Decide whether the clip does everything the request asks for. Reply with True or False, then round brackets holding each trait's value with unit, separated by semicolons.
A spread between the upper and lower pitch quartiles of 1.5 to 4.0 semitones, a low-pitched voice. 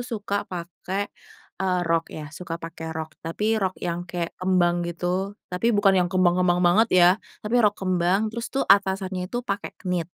False (2.5 semitones; 185 Hz)